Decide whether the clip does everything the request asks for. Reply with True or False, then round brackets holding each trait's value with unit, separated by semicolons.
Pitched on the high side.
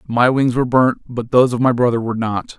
False (120 Hz)